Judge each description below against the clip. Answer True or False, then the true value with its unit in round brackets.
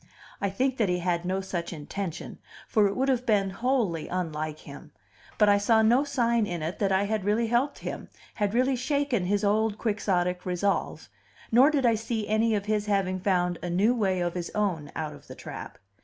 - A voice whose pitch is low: False (205 Hz)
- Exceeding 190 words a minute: True (205 wpm)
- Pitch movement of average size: True (4.3 semitones)